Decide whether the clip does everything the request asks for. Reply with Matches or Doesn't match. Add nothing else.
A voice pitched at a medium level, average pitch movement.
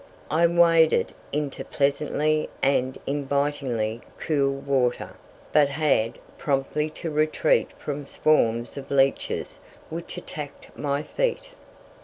Doesn't match